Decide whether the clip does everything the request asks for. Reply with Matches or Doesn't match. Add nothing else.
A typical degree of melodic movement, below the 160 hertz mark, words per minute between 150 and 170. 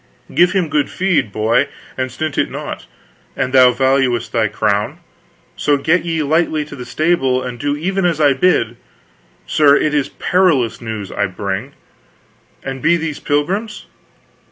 Matches